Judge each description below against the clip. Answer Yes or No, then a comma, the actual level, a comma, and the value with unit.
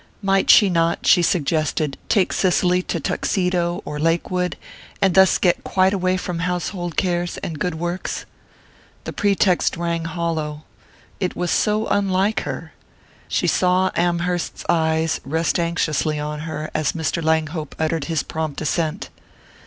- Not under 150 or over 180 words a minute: No, average, 140 wpm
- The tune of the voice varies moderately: No, narrow, 2.3 semitones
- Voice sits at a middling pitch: Yes, medium, 170 Hz